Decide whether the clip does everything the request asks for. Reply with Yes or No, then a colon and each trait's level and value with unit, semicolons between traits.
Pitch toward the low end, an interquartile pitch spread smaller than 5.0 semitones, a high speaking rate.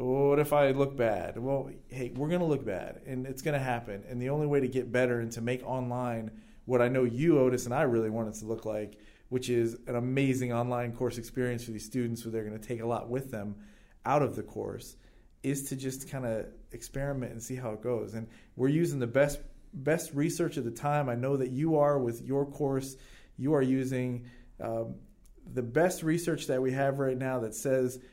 Yes: low, 125 Hz; average, 2.8 semitones; fast, 220 wpm